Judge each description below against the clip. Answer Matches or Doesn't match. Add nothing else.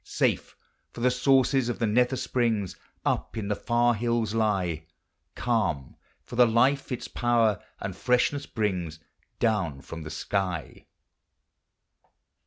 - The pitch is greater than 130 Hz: Doesn't match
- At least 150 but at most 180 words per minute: Doesn't match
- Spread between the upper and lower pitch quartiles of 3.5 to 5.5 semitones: Matches